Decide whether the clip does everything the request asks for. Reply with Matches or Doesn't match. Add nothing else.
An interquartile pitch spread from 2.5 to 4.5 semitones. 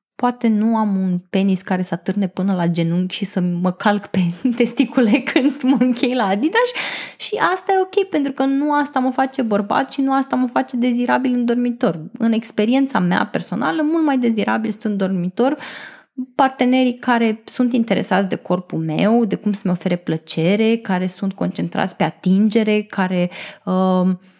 Doesn't match